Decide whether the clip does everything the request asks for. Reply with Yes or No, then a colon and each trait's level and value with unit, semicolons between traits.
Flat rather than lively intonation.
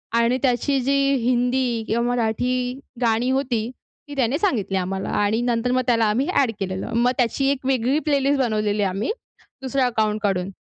No: average, 3.3 semitones